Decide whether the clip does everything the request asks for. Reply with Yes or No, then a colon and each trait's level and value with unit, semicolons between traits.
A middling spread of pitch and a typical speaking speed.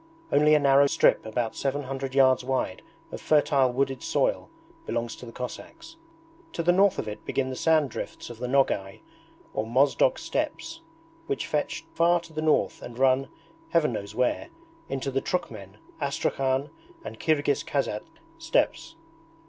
Yes: average, 3.9 semitones; average, 155 wpm